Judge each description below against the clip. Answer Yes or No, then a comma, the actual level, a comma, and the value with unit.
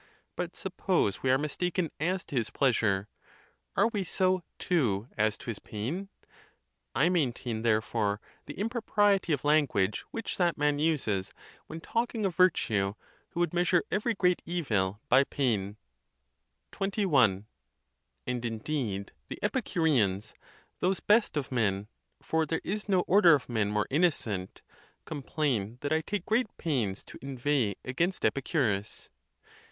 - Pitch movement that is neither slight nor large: No, wide, 8.5 semitones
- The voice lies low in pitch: No, medium, 145 Hz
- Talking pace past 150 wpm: No, slow, 135 wpm